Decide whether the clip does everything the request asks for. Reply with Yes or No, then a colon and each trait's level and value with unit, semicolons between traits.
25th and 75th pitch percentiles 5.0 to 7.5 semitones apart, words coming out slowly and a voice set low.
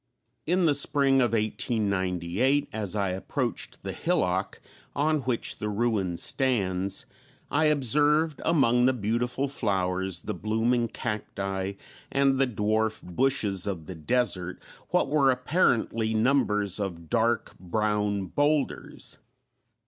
Yes: wide, 5.5 semitones; slow, 120 wpm; low, 110 Hz